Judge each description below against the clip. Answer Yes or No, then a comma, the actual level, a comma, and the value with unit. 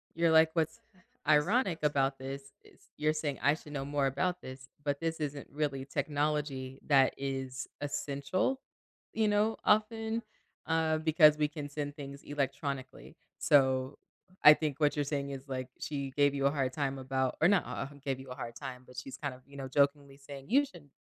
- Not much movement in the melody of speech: Yes, narrow, 2.2 semitones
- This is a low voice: No, medium, 145 Hz